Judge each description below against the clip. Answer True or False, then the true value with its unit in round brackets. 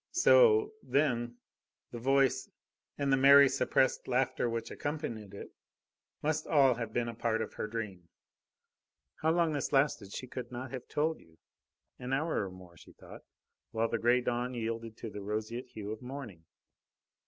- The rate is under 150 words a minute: False (165 wpm)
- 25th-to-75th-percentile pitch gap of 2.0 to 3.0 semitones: False (3.8 semitones)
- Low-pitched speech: True (120 Hz)